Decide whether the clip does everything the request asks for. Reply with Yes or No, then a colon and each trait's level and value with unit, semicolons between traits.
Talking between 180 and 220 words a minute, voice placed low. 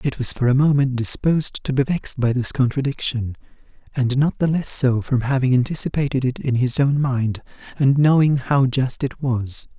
Yes: average, 190 wpm; low, 130 Hz